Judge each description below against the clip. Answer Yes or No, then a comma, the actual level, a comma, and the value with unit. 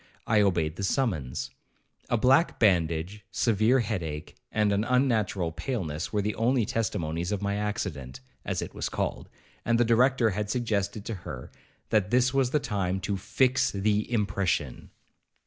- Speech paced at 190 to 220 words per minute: No, average, 160 wpm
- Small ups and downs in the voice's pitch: No, average, 4.3 semitones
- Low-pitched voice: Yes, low, 105 Hz